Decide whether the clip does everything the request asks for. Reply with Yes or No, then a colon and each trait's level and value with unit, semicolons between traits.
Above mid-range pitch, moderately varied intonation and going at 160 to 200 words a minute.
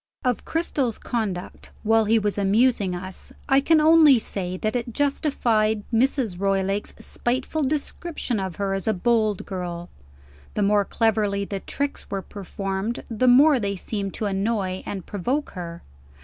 No: high, 215 Hz; average, 4.3 semitones; average, 150 wpm